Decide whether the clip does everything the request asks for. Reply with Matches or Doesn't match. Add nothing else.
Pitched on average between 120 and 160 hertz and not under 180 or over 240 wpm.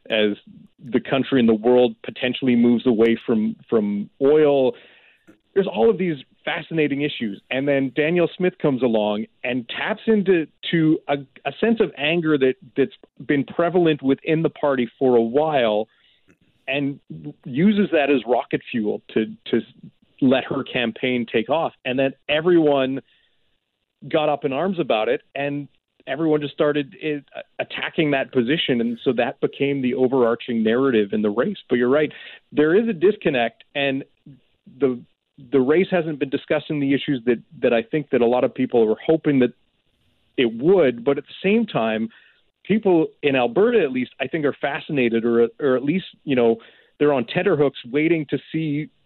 Doesn't match